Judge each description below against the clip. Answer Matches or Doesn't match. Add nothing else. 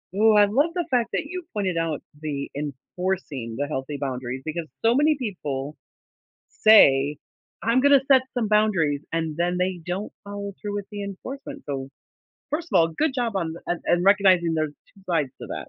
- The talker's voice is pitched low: Doesn't match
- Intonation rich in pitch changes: Matches